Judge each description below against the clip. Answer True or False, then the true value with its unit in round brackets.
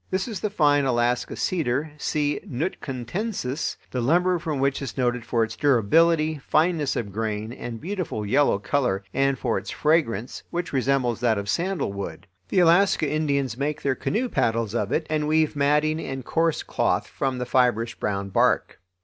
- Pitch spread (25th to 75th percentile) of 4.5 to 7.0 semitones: True (4.9 semitones)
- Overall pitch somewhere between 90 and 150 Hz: True (140 Hz)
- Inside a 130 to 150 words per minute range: False (165 wpm)